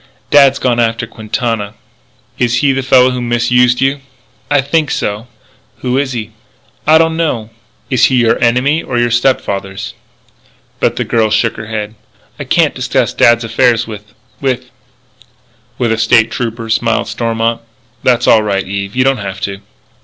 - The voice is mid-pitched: No, low, 120 Hz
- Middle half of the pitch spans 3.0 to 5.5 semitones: No, narrow, 2.5 semitones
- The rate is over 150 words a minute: Yes, average, 165 wpm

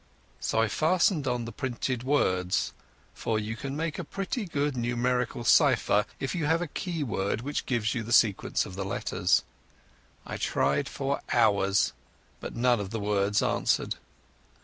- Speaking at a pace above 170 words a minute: No, average, 165 wpm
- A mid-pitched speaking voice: No, low, 120 Hz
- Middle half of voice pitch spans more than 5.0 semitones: Yes, wide, 5.5 semitones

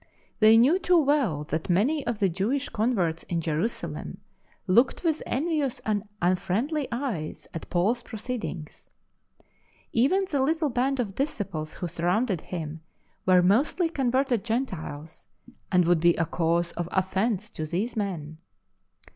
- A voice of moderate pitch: No, high, 210 Hz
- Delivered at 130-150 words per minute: Yes, average, 145 wpm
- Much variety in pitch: Yes, wide, 7.3 semitones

